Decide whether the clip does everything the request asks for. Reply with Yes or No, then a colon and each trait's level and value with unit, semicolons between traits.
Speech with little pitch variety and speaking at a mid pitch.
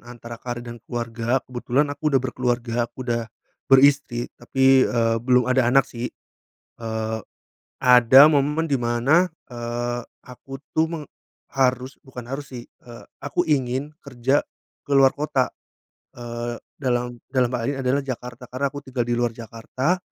No: narrow, 2.3 semitones; low, 125 Hz